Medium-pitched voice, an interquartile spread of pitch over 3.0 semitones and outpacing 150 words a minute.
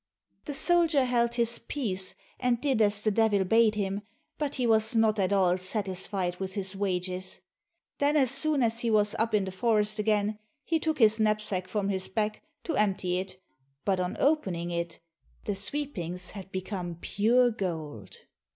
No: high, 210 Hz; average, 3.9 semitones; average, 170 wpm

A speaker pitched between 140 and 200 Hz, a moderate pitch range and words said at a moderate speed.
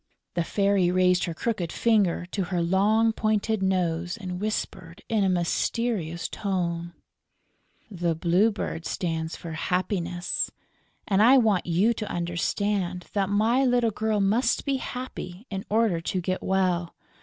Yes: high, 190 Hz; average, 3.7 semitones; average, 145 wpm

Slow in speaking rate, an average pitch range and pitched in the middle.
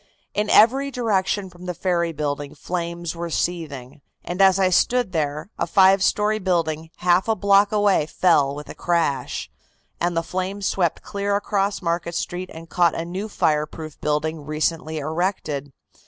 No: average, 160 wpm; average, 3.6 semitones; medium, 175 Hz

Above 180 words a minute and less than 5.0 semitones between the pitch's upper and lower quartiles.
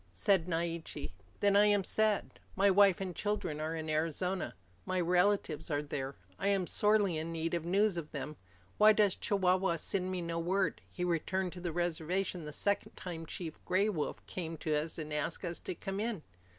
Yes: average, 190 wpm; average, 3.3 semitones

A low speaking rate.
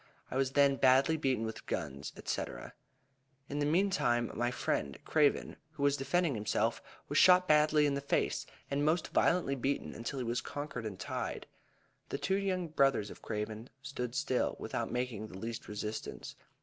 No: average, 170 wpm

